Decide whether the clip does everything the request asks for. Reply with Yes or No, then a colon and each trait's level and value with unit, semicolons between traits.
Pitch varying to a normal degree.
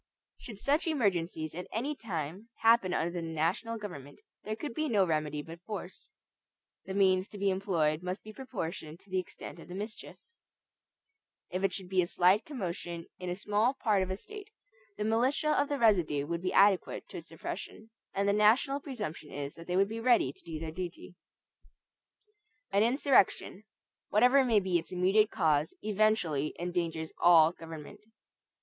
Yes: average, 4.6 semitones